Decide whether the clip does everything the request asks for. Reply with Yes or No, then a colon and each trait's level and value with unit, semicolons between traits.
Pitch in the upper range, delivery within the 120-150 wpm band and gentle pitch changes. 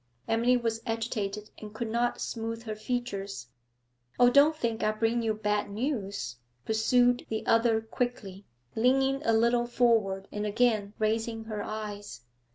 Yes: high, 225 Hz; average, 145 wpm; narrow, 2.3 semitones